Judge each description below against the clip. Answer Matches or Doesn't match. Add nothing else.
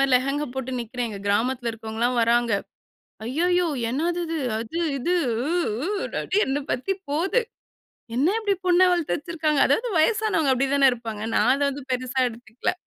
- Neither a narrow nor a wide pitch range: Doesn't match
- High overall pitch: Matches